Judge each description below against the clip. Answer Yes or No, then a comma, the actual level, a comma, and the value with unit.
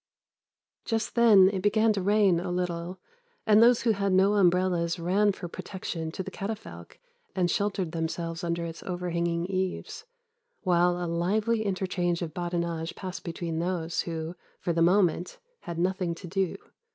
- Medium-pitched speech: Yes, medium, 180 Hz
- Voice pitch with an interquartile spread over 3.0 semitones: No, narrow, 2.6 semitones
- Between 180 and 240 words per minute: No, average, 155 wpm